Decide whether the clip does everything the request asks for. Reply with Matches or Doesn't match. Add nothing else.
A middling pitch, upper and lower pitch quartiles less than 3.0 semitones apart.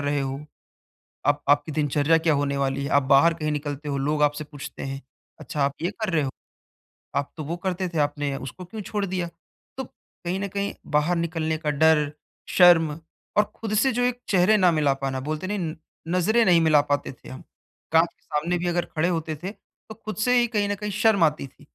Doesn't match